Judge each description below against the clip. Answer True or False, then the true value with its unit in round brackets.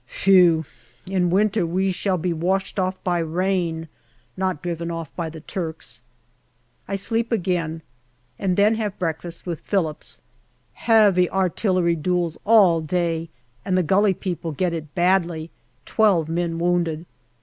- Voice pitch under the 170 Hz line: False (175 Hz)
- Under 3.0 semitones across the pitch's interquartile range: True (2.5 semitones)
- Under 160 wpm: True (140 wpm)